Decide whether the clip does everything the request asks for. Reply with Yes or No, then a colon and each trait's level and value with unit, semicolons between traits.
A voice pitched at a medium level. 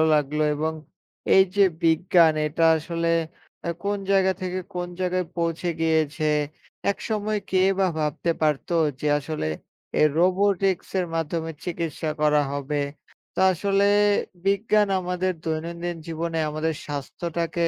Yes: medium, 170 Hz